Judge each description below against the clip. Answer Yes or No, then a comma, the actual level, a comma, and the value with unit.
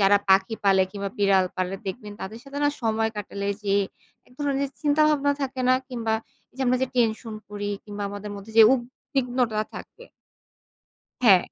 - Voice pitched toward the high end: Yes, high, 220 Hz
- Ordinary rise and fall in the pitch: Yes, average, 4.3 semitones